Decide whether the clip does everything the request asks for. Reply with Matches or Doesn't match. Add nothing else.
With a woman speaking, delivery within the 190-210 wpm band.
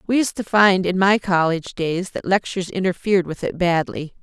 Matches